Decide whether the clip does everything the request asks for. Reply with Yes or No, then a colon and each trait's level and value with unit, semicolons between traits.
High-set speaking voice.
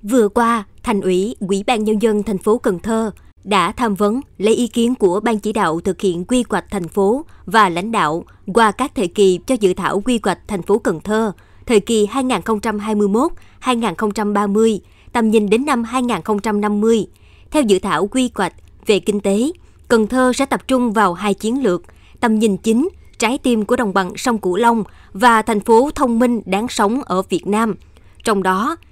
Yes: high, 220 Hz